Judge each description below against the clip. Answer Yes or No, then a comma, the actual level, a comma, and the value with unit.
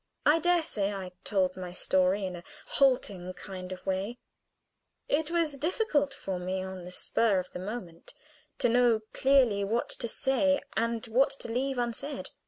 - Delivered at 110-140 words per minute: No, average, 170 wpm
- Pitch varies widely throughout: Yes, wide, 6.4 semitones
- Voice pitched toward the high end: Yes, high, 225 Hz